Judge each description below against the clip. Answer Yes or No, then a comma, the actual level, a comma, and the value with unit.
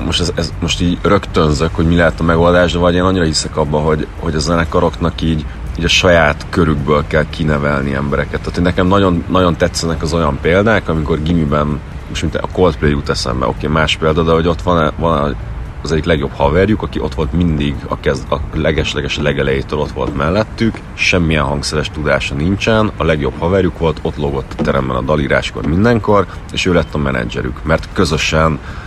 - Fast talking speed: Yes, fast, 195 wpm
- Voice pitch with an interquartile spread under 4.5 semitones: Yes, average, 2.7 semitones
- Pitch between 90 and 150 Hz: No, very low, 80 Hz